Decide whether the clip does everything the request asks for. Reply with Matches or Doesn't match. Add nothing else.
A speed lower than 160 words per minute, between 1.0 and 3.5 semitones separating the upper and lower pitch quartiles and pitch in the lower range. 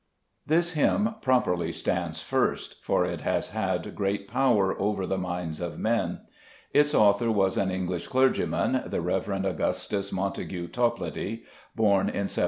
Doesn't match